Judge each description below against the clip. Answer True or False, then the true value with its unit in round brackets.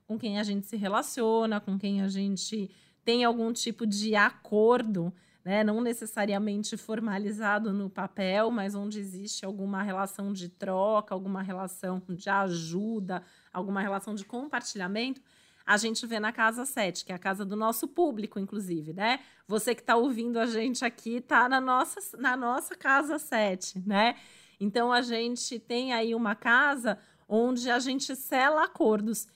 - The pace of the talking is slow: False (160 wpm)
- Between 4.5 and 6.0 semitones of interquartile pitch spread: False (3.3 semitones)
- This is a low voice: False (215 Hz)